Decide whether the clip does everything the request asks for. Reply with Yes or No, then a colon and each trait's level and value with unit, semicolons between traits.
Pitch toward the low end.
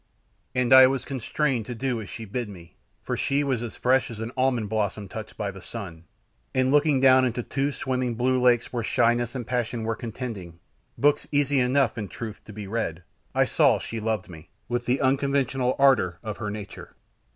Yes: low, 120 Hz